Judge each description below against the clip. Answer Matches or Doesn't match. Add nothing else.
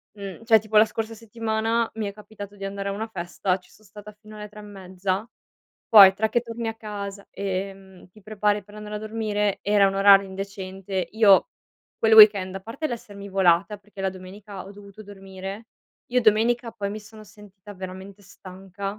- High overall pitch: Matches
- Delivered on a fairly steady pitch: Matches